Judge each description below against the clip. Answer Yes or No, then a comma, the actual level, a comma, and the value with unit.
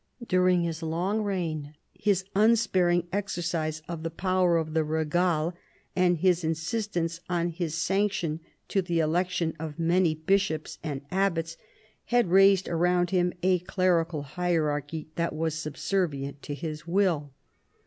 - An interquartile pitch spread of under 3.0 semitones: Yes, narrow, 2.6 semitones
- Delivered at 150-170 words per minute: No, slow, 135 wpm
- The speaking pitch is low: No, medium, 170 Hz